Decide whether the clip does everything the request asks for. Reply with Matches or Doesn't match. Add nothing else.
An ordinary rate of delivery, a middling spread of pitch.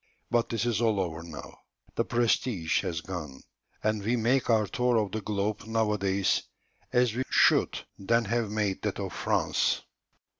Matches